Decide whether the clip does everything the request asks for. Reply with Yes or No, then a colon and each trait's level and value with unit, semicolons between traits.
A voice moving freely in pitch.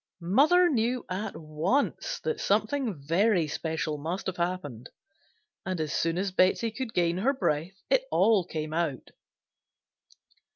Yes: wide, 6.0 semitones